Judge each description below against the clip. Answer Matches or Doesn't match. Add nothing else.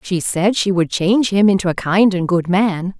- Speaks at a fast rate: Matches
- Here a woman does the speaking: Matches